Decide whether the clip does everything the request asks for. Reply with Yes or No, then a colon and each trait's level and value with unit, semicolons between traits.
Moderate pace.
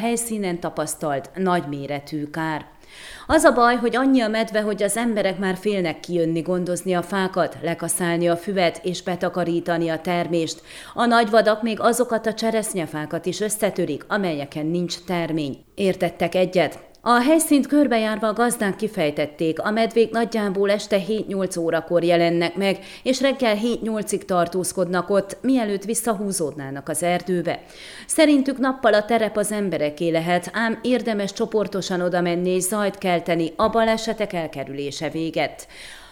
Yes: average, 135 wpm